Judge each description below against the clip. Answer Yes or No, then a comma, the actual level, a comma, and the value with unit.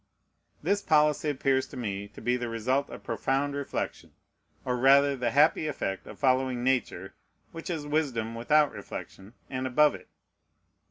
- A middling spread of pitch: Yes, average, 3.3 semitones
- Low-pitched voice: Yes, low, 130 Hz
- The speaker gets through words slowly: No, average, 155 wpm